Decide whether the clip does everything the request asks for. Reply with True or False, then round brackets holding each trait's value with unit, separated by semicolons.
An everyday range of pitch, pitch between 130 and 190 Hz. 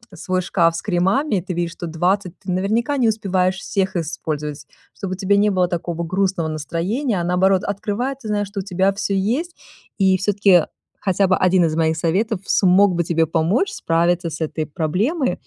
True (3.1 semitones; 185 Hz)